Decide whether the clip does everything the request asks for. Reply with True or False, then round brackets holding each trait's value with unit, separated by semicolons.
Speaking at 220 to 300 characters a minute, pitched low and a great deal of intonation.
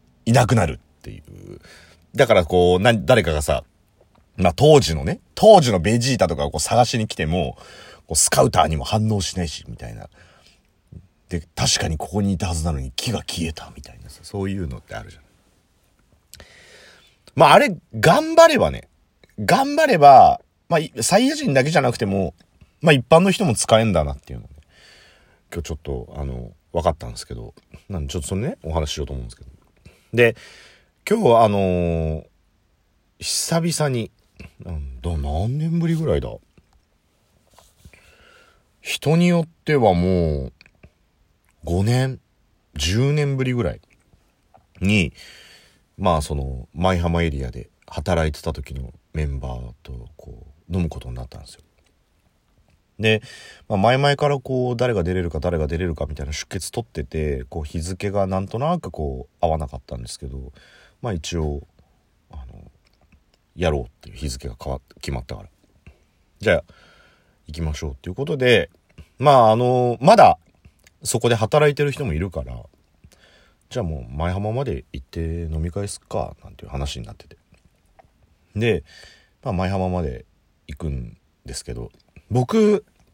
True (295 characters per minute; 90 Hz; 6.4 semitones)